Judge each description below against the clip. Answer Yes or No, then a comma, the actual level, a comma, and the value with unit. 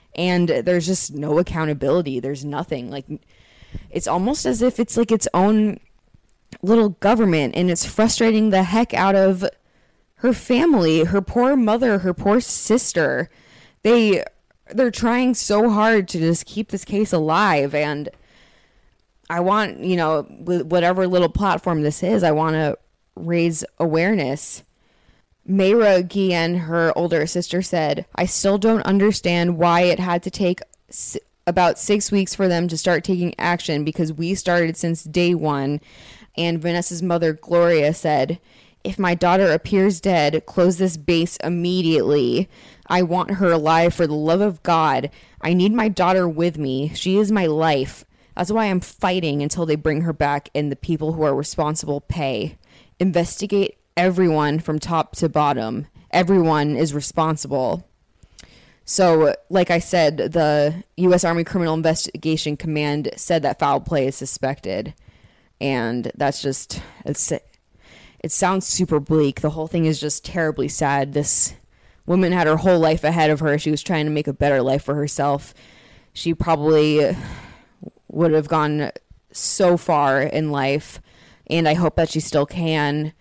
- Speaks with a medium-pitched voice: Yes, medium, 170 Hz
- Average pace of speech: Yes, average, 155 wpm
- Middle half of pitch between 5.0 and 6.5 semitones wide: No, average, 3.6 semitones